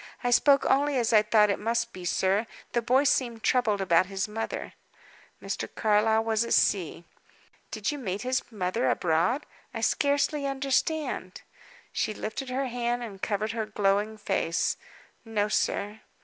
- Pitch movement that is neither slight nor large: Yes, average, 3.5 semitones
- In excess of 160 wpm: No, average, 155 wpm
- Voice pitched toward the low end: No, high, 225 Hz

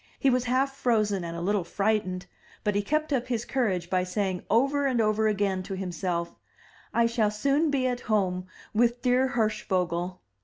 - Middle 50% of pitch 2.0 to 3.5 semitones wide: No, average, 5.0 semitones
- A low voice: No, high, 215 Hz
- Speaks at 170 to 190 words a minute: Yes, average, 180 wpm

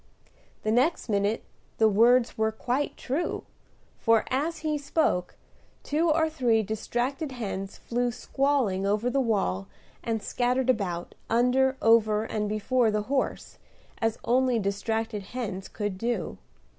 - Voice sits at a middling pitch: No, high, 230 Hz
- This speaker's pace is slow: Yes, slow, 130 wpm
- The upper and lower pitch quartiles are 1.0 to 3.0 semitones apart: No, average, 3.6 semitones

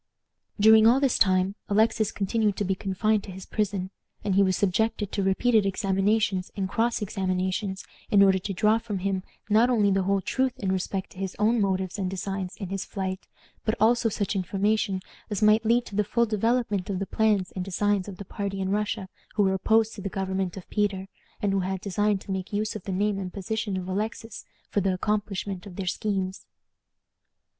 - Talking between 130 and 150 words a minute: No, average, 200 wpm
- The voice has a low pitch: No, high, 200 Hz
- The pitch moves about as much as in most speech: No, narrow, 2.1 semitones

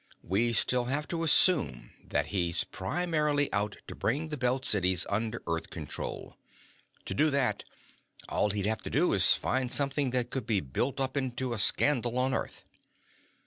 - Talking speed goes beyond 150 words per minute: Yes, average, 170 wpm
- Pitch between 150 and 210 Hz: No, low, 125 Hz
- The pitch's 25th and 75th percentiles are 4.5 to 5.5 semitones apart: Yes, average, 5.1 semitones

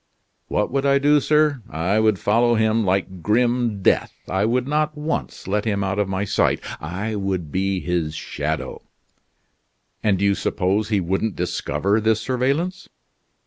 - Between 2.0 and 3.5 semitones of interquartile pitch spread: No, average, 4.5 semitones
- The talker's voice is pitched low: Yes, low, 105 Hz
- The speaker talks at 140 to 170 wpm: Yes, average, 160 wpm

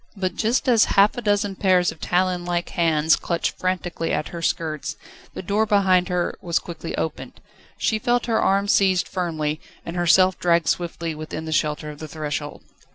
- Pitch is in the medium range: Yes, medium, 175 Hz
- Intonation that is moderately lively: Yes, average, 3.3 semitones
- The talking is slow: No, average, 180 wpm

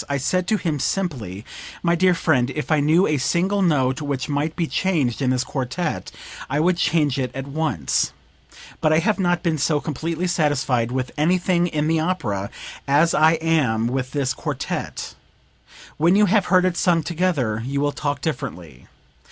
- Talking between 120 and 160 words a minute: No, average, 175 wpm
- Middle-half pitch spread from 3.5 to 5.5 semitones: Yes, average, 4.6 semitones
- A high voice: No, medium, 155 Hz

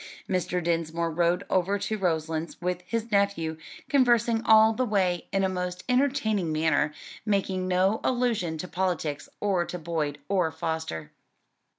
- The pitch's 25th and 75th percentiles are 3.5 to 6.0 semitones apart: Yes, average, 4.1 semitones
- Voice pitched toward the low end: No, medium, 180 Hz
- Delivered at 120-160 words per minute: Yes, average, 145 wpm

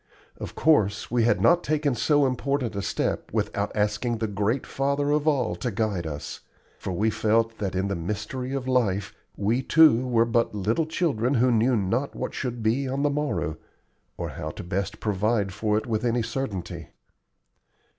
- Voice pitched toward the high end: No, low, 115 Hz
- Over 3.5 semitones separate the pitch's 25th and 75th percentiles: Yes, average, 4.4 semitones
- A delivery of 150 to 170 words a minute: No, average, 180 wpm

